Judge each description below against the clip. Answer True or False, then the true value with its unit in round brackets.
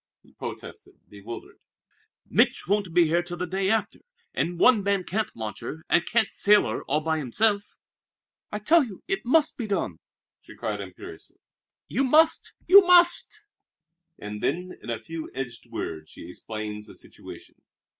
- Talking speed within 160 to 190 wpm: True (165 wpm)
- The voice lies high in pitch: False (180 Hz)